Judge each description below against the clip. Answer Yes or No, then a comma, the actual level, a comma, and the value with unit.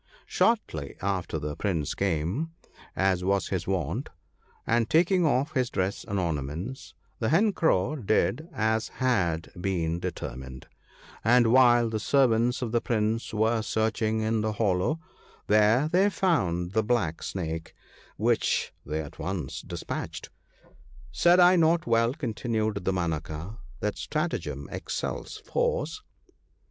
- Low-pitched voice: Yes, low, 110 Hz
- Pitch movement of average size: No, wide, 6.3 semitones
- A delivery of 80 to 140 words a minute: Yes, slow, 135 wpm